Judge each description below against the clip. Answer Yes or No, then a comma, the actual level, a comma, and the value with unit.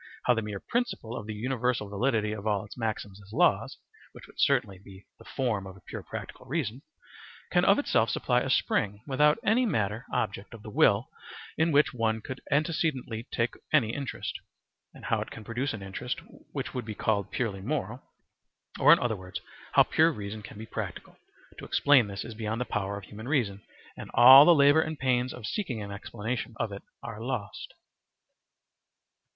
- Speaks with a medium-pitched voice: No, low, 115 Hz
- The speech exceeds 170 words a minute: Yes, average, 190 wpm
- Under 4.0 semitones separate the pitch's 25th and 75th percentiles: No, average, 4.3 semitones